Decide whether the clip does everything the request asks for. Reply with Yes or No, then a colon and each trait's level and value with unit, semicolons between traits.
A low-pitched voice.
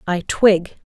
No: high, 190 Hz